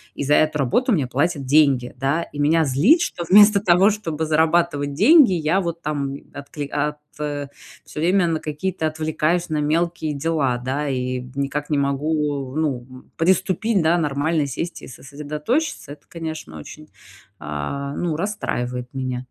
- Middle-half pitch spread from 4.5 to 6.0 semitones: No, average, 3.3 semitones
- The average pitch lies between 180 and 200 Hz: No, medium, 150 Hz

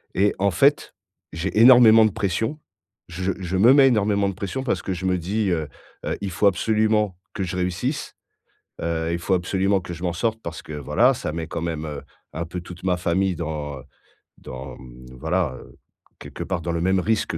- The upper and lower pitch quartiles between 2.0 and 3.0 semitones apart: No, average, 3.6 semitones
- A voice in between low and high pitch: No, very low, 90 Hz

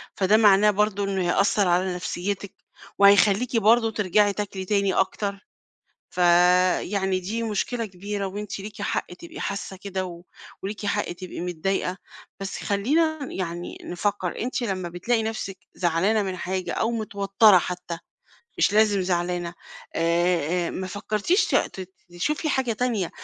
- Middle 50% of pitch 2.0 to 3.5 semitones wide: Yes, average, 2.7 semitones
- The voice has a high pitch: Yes, high, 195 Hz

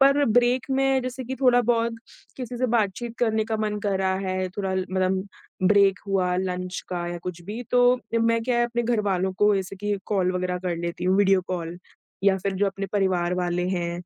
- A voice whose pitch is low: No, high, 195 Hz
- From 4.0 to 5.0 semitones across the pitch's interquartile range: Yes, average, 4.3 semitones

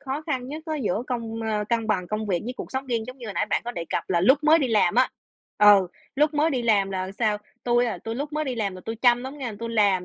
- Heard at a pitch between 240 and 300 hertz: No, high, 230 Hz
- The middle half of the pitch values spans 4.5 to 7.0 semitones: No, average, 4.0 semitones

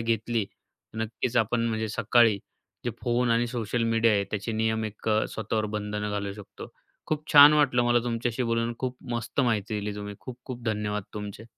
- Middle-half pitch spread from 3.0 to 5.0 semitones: No, narrow, 2.4 semitones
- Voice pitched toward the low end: Yes, low, 115 Hz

